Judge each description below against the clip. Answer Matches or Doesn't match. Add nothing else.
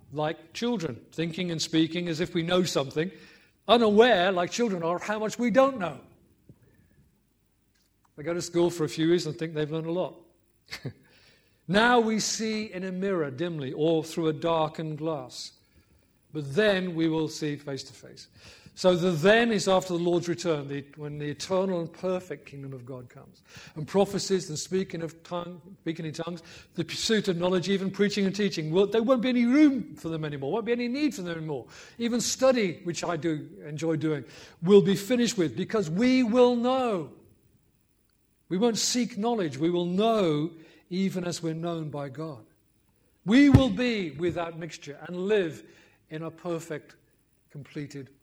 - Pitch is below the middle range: Doesn't match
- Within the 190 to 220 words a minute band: Doesn't match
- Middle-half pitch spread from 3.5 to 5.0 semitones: Matches